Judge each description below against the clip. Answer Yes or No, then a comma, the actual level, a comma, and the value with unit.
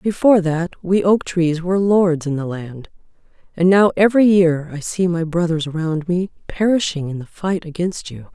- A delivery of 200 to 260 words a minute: No, average, 185 wpm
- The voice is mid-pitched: Yes, medium, 175 Hz